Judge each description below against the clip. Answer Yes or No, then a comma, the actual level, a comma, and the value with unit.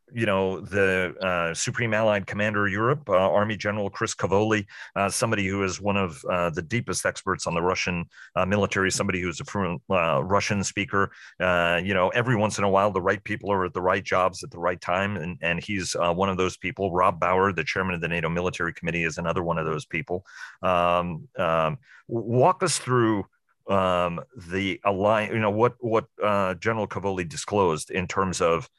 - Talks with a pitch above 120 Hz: No, very low, 95 Hz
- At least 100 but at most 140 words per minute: No, fast, 205 wpm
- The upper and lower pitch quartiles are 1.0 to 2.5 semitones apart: No, average, 2.9 semitones